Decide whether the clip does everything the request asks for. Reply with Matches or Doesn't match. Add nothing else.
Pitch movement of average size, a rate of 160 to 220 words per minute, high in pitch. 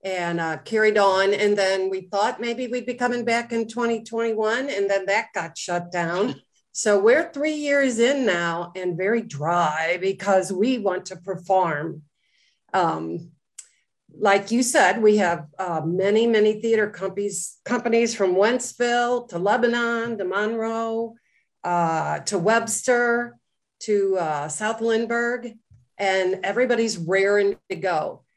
Doesn't match